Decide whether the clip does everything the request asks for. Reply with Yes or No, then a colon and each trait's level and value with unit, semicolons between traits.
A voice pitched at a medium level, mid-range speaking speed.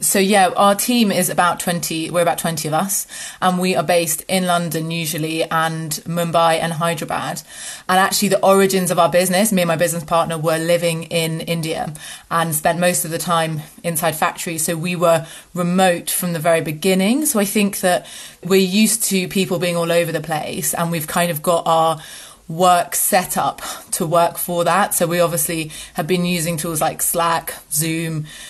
Yes: medium, 170 Hz; average, 190 wpm